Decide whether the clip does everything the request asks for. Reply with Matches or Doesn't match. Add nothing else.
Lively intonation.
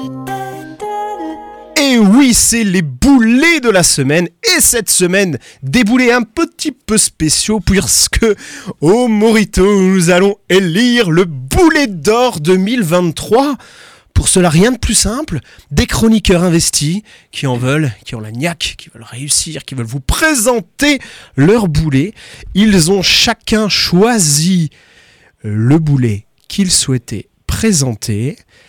Matches